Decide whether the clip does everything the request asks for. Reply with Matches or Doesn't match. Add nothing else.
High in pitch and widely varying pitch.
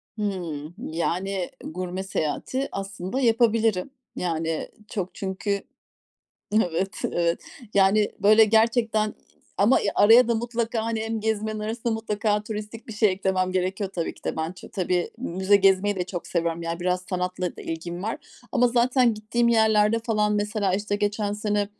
Doesn't match